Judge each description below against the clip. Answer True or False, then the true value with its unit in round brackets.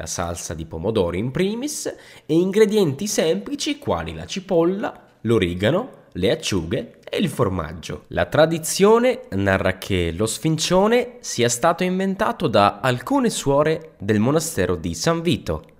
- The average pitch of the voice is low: False (160 Hz)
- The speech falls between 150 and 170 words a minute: False (135 wpm)